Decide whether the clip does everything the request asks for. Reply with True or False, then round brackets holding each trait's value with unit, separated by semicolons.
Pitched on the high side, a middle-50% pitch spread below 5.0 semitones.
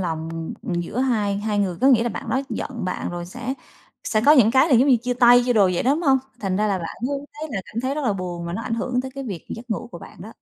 False (230 Hz; 5.3 semitones)